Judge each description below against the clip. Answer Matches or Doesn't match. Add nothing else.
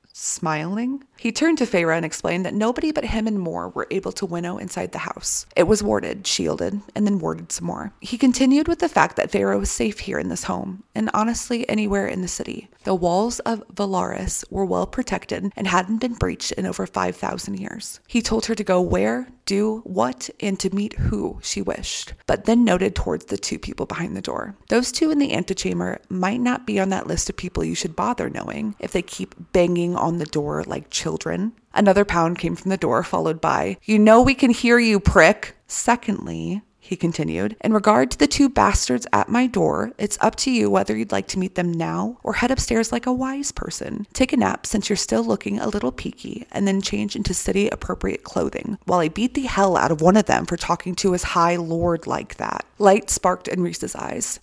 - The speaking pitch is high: Matches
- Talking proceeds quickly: Matches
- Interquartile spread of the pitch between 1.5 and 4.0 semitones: Doesn't match